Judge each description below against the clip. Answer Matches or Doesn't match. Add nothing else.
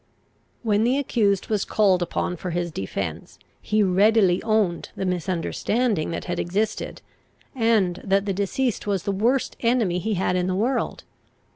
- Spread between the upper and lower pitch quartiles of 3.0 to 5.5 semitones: Matches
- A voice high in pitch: Matches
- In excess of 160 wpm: Doesn't match